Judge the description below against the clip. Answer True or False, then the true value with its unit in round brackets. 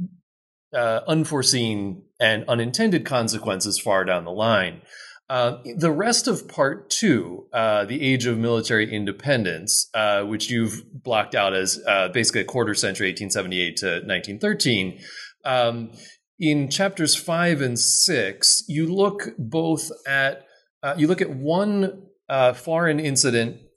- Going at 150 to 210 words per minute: False (135 wpm)